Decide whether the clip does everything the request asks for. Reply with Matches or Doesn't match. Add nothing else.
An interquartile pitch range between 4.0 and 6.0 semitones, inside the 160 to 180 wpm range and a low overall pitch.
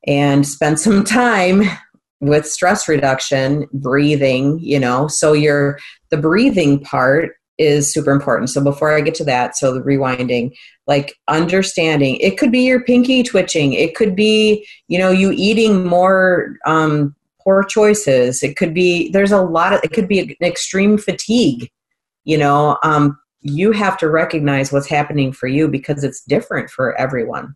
Doesn't match